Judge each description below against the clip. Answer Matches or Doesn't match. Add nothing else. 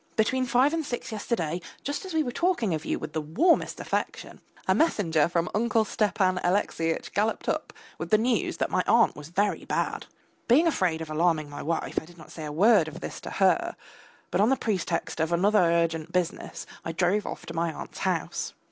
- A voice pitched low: Doesn't match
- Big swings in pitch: Matches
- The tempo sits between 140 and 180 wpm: Doesn't match